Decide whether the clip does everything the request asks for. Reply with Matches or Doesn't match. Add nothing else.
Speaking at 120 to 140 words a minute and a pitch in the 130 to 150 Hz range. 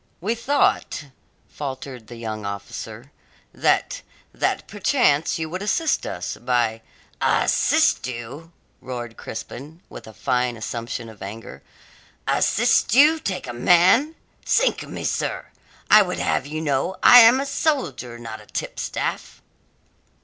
Matches